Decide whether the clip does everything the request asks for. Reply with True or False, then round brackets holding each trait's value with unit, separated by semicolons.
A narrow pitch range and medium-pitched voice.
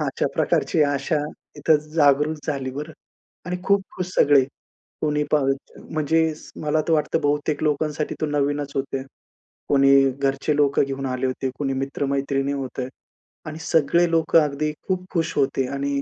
True (2.1 semitones; 145 Hz)